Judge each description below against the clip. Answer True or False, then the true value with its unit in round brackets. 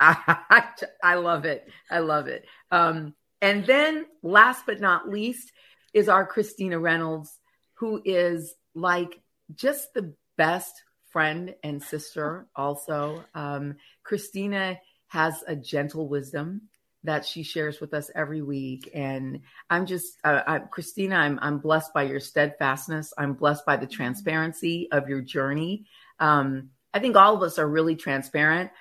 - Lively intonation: False (3.9 semitones)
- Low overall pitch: False (160 Hz)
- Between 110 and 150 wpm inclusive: True (145 wpm)